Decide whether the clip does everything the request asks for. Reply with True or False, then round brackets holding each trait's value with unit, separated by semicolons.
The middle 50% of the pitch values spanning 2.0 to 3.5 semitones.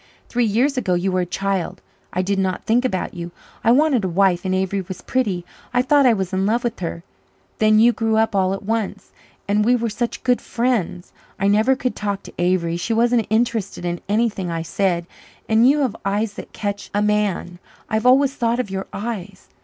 False (3.9 semitones)